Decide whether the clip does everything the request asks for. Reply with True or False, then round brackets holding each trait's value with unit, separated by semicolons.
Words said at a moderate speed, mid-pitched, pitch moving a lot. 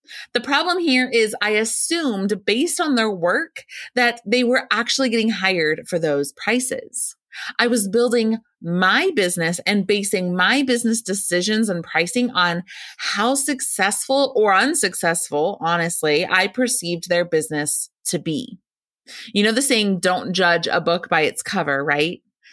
False (145 wpm; 210 Hz; 5.7 semitones)